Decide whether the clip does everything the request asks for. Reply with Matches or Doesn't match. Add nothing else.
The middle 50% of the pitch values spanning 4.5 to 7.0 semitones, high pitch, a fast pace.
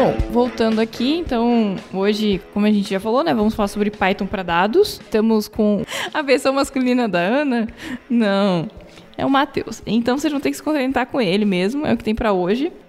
Doesn't match